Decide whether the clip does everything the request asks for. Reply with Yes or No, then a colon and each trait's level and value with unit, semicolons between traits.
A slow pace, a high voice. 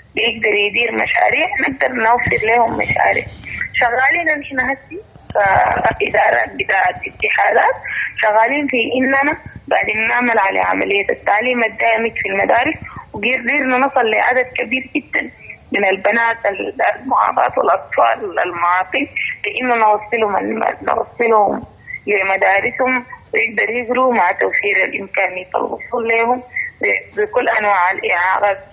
Yes: slow, 100 wpm; high, 245 Hz